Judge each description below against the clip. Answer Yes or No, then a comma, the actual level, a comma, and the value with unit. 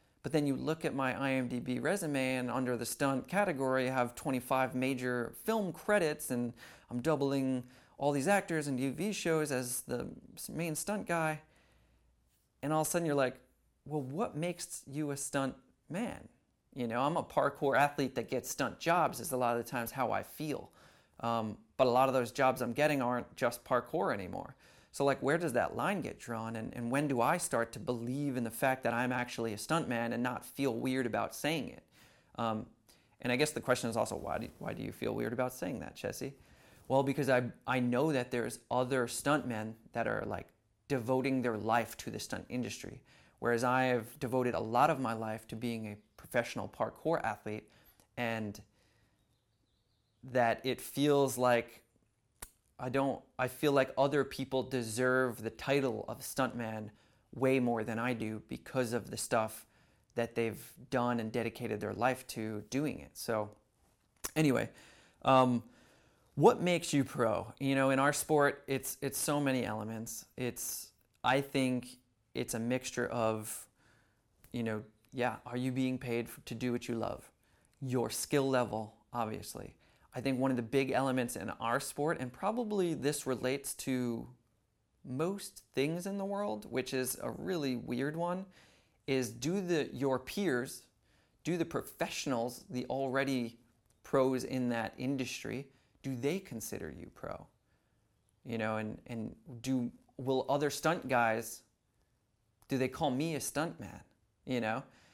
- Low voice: Yes, low, 125 Hz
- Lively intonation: No, average, 3.0 semitones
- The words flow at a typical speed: Yes, average, 170 wpm